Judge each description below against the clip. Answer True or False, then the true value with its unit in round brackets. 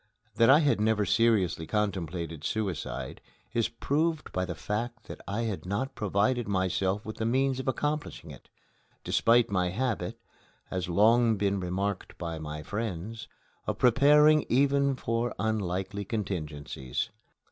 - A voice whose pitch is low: True (105 Hz)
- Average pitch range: True (4.5 semitones)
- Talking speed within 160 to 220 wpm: False (135 wpm)